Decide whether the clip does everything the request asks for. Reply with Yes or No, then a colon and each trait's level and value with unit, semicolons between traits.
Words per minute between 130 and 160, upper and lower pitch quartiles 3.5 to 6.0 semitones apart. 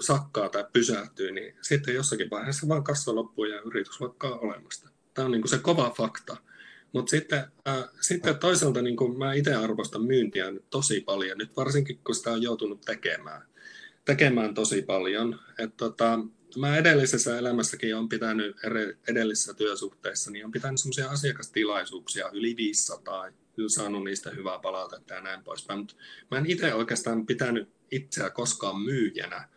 Yes: fast, 155 wpm; average, 4.3 semitones